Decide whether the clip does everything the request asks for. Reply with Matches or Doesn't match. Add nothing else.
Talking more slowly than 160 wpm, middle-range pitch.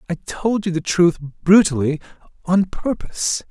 Matches